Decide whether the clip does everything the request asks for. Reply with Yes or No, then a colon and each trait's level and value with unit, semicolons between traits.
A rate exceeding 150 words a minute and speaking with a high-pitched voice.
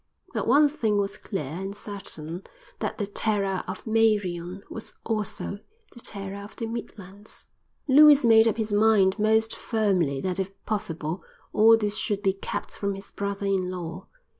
Yes: average, 165 wpm; high, 205 Hz